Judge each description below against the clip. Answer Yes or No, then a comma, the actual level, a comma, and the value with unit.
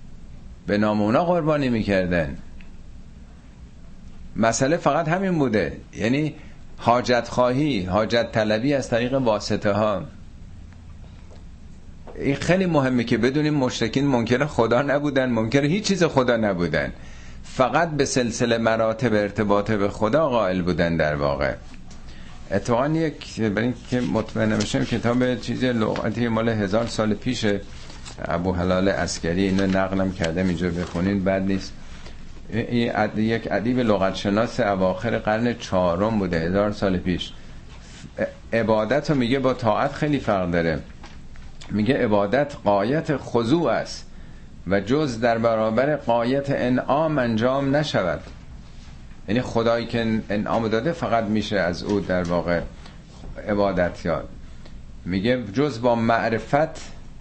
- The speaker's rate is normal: Yes, average, 120 wpm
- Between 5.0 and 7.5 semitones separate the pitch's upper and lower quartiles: Yes, wide, 5.5 semitones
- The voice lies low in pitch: Yes, low, 110 Hz